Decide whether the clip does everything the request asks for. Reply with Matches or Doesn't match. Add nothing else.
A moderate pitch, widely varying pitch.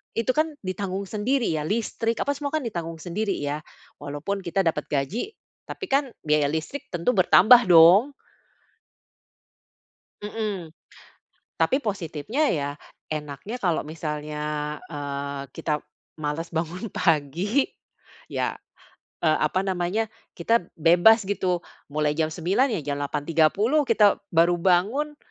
Matches